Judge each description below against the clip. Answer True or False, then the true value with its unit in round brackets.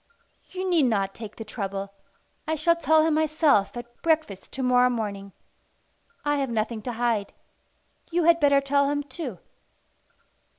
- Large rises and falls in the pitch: True (6.1 semitones)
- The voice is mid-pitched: False (260 Hz)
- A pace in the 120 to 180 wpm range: True (155 wpm)